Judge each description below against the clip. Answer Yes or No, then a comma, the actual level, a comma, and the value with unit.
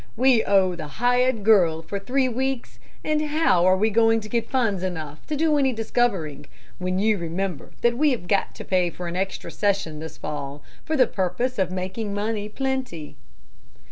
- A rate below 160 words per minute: No, average, 185 wpm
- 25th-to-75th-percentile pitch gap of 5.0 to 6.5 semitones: Yes, wide, 5.6 semitones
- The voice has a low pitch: No, high, 205 Hz